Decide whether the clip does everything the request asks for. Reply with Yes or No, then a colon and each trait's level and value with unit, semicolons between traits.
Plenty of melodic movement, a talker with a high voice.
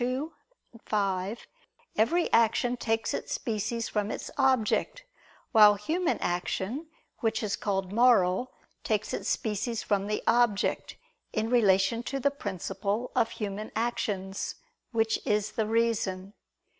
No: average, 2.9 semitones; high, 220 Hz